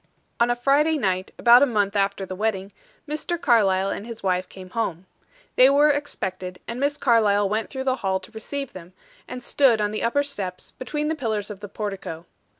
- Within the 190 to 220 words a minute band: Yes, average, 200 wpm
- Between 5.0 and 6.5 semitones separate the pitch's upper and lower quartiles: Yes, wide, 5.6 semitones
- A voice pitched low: No, high, 220 Hz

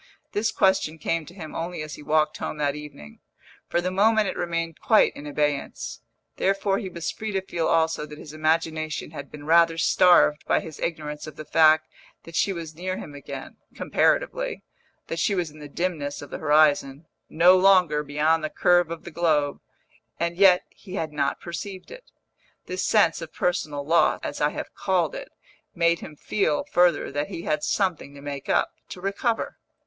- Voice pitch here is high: No, medium, 165 Hz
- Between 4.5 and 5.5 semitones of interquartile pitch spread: No, average, 3.4 semitones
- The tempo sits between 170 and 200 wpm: Yes, average, 190 wpm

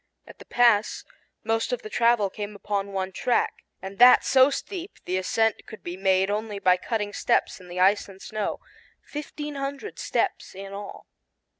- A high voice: Yes, high, 210 Hz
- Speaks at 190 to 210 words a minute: No, average, 175 wpm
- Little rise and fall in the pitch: No, average, 3.8 semitones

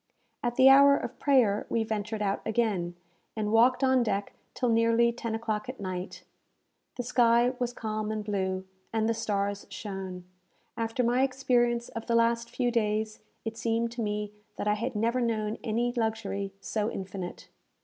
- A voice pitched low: No, high, 225 Hz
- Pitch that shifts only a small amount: Yes, narrow, 2.3 semitones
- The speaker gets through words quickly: No, average, 170 wpm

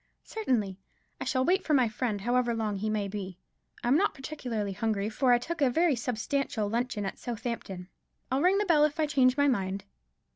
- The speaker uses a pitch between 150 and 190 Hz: No, high, 245 Hz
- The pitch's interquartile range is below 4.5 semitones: No, average, 5.2 semitones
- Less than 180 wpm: No, average, 195 wpm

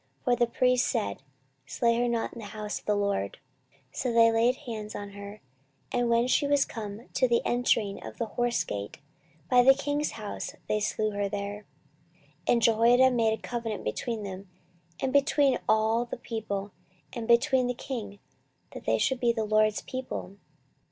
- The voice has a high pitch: Yes, high, 230 Hz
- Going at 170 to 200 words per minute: Yes, average, 185 wpm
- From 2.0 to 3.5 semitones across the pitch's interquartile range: Yes, average, 3.0 semitones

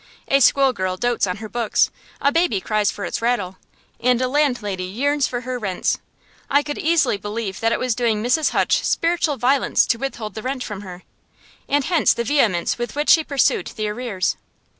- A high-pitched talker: Yes, high, 240 Hz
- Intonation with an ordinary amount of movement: Yes, average, 4.9 semitones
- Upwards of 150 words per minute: Yes, average, 195 wpm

